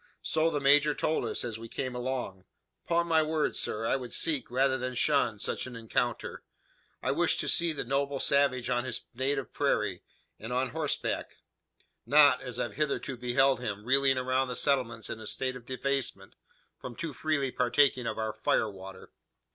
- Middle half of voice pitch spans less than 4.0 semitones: Yes, average, 2.8 semitones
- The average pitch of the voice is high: No, low, 130 Hz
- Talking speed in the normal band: Yes, average, 180 wpm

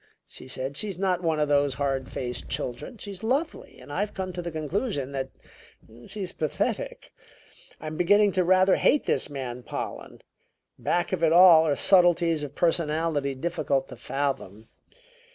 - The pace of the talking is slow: No, average, 155 wpm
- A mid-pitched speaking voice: Yes, medium, 160 Hz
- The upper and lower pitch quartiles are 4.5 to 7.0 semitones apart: Yes, average, 5.0 semitones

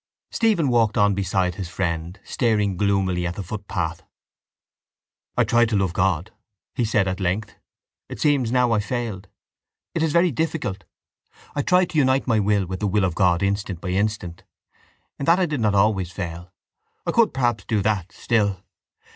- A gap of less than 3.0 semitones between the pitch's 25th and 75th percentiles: No, average, 4.4 semitones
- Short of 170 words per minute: No, average, 175 wpm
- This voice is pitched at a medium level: No, low, 100 Hz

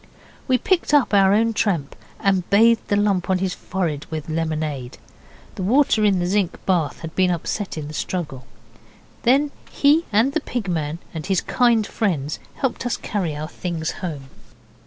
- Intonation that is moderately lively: No, wide, 5.7 semitones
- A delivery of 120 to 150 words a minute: No, average, 175 wpm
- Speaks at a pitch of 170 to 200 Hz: Yes, high, 190 Hz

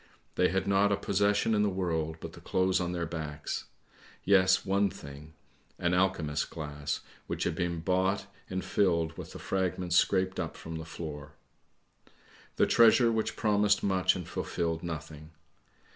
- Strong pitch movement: No, average, 3.3 semitones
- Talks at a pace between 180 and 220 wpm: No, average, 160 wpm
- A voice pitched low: Yes, very low, 90 Hz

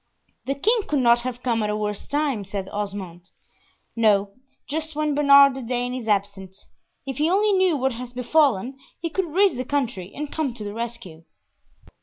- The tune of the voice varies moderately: No, wide, 6.0 semitones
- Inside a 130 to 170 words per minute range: No, average, 185 wpm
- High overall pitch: Yes, very high, 250 Hz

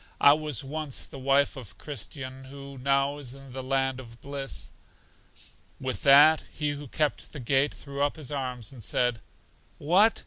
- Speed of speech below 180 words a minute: Yes, average, 170 wpm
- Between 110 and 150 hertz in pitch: Yes, medium, 140 Hz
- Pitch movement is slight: Yes, narrow, 1.9 semitones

